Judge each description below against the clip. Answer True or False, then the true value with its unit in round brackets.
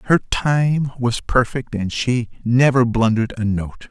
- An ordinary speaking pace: True (155 wpm)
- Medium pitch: False (120 Hz)